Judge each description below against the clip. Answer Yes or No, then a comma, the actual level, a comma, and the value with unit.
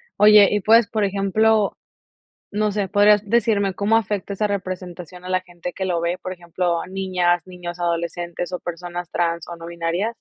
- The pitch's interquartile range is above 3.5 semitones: No, average, 2.7 semitones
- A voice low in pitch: No, medium, 185 Hz